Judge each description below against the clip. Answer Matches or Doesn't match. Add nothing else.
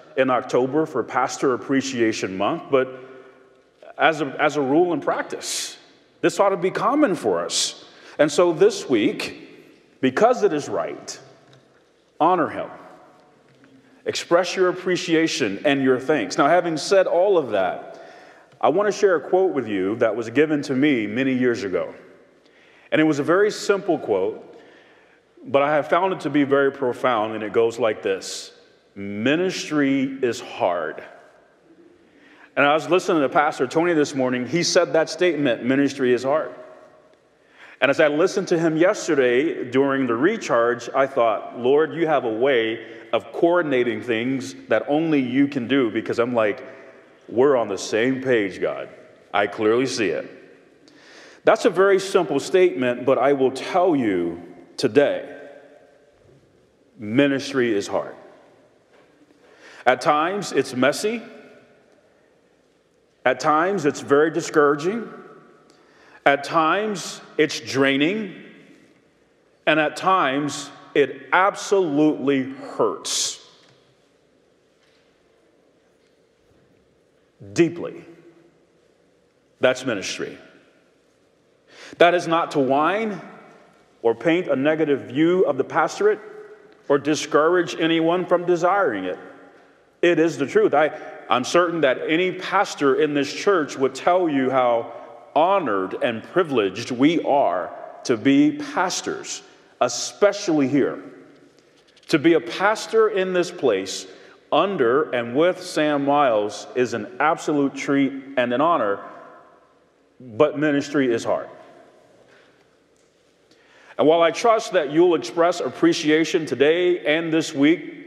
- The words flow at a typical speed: Doesn't match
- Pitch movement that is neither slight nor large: Doesn't match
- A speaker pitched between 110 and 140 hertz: Doesn't match